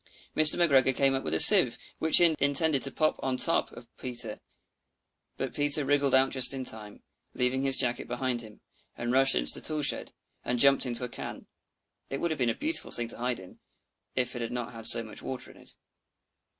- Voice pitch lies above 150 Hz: No, low, 130 Hz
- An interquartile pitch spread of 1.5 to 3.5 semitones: Yes, average, 2.7 semitones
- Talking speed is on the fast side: Yes, fast, 215 wpm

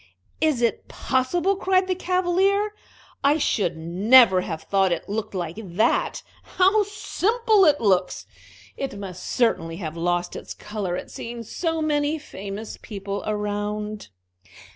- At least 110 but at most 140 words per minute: Yes, slow, 135 wpm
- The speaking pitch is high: Yes, high, 220 Hz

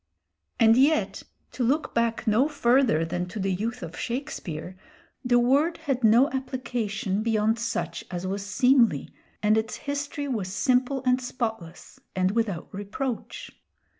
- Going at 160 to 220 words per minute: No, average, 140 wpm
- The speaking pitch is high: Yes, high, 230 Hz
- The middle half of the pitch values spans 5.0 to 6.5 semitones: No, average, 4.4 semitones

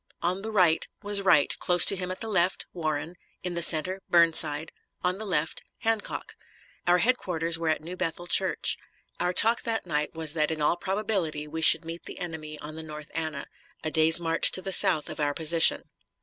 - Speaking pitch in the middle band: Yes, medium, 165 Hz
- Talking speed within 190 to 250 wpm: Yes, average, 200 wpm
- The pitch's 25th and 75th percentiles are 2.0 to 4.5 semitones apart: Yes, average, 2.8 semitones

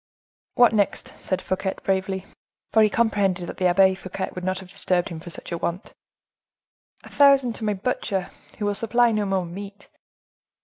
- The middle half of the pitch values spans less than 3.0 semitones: Yes, narrow, 2.4 semitones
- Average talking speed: Yes, average, 180 wpm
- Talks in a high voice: Yes, high, 195 Hz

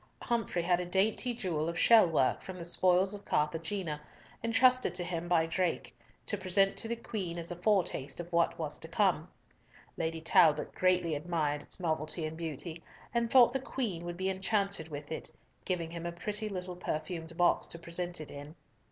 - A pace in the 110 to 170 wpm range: No, average, 185 wpm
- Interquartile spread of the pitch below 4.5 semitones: Yes, average, 2.9 semitones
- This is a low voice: No, medium, 175 Hz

